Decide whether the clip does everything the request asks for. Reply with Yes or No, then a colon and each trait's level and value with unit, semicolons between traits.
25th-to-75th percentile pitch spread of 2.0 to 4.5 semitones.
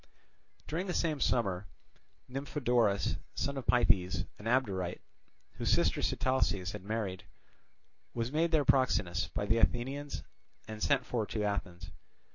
No: average, 5.2 semitones